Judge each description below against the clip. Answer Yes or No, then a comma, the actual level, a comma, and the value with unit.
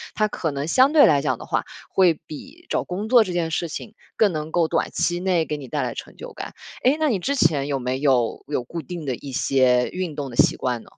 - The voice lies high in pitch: No, medium, 160 Hz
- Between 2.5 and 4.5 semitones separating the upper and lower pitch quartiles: No, wide, 5.6 semitones